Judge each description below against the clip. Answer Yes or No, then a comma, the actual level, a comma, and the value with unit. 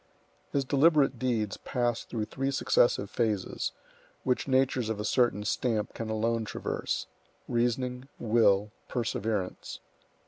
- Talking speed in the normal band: No, slow, 110 wpm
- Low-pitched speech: Yes, low, 120 Hz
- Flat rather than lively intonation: No, average, 3.0 semitones